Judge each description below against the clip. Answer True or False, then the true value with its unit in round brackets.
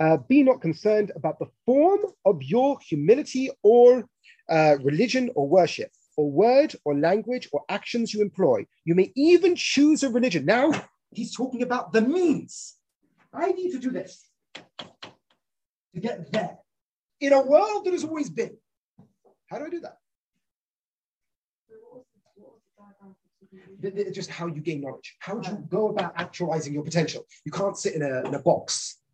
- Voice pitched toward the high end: True (210 Hz)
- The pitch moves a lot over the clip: True (7.9 semitones)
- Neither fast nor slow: True (155 wpm)